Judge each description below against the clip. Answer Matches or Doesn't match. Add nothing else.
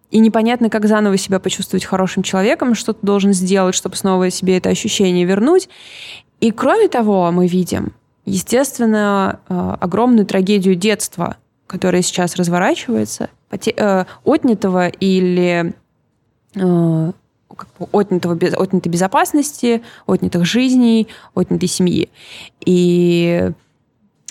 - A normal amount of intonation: Matches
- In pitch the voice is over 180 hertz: Matches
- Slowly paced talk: Matches